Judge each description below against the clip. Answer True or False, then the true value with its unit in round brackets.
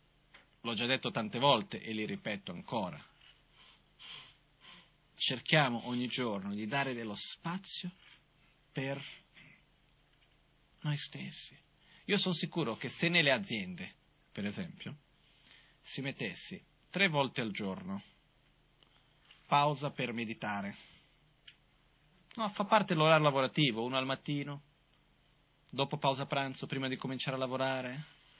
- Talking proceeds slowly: True (110 wpm)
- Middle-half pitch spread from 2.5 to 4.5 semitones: True (3.3 semitones)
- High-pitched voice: False (145 Hz)